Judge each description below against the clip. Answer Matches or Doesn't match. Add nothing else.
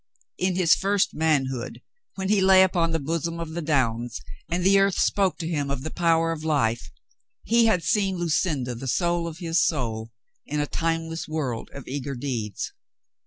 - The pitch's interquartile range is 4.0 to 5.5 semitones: Matches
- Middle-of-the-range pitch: Matches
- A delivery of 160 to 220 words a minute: Matches